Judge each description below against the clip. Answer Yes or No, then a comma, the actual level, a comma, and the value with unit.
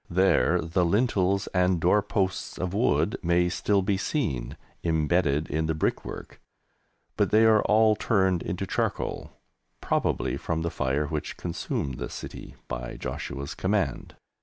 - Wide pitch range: No, average, 3.8 semitones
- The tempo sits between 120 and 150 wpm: Yes, average, 140 wpm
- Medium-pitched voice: No, very low, 90 Hz